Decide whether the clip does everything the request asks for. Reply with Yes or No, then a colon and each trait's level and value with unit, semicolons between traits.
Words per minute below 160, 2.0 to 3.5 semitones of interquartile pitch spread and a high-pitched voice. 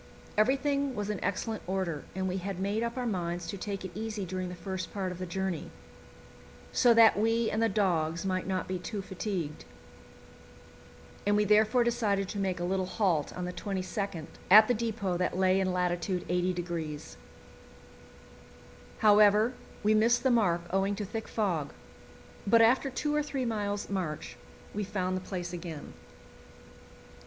No: average, 165 wpm; average, 3.1 semitones; high, 195 Hz